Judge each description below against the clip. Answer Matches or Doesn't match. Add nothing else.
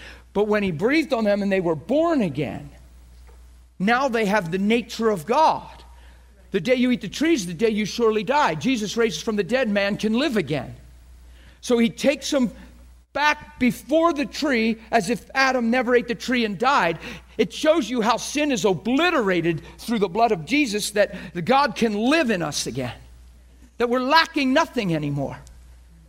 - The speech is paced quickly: Doesn't match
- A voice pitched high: Matches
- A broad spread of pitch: Matches